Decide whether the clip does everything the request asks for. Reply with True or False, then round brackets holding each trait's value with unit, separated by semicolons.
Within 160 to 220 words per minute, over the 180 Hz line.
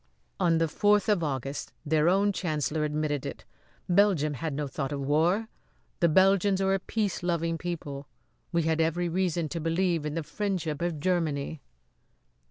False (165 wpm; 165 Hz)